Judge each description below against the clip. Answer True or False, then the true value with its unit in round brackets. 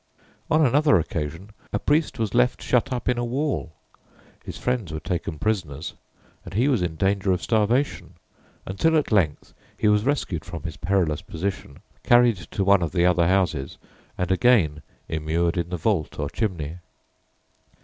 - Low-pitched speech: True (95 Hz)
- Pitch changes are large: True (6.5 semitones)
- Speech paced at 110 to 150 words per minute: False (165 wpm)